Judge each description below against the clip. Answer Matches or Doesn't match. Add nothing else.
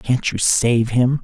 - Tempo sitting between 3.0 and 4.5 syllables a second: Matches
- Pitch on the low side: Matches